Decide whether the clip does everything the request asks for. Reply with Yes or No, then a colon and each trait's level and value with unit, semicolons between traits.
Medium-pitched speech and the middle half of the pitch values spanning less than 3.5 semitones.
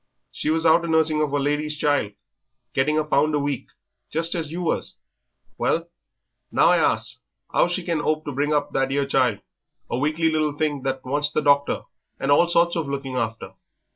Yes: medium, 150 Hz; narrow, 2.6 semitones